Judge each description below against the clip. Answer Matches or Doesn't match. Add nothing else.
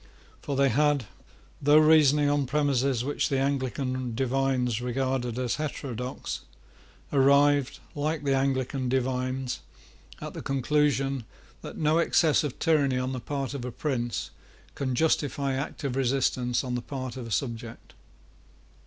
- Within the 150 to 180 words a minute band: Doesn't match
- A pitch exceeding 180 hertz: Doesn't match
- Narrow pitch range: Matches